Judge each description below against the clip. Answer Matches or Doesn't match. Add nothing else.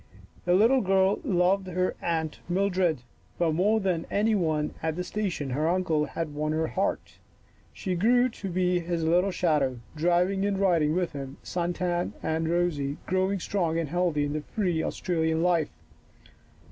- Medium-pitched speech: Matches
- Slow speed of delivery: Doesn't match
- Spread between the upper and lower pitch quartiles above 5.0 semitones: Doesn't match